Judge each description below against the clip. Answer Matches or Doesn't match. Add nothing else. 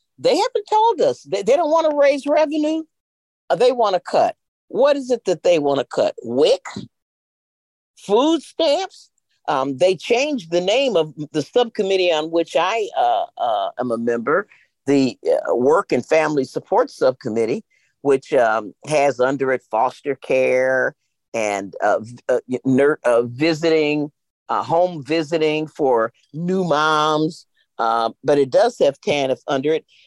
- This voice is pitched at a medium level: Matches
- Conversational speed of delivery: Matches